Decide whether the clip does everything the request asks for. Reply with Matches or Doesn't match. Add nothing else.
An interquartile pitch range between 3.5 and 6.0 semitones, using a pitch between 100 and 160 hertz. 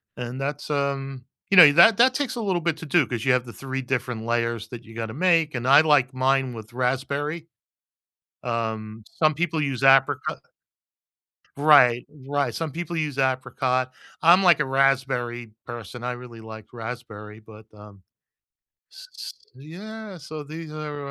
Matches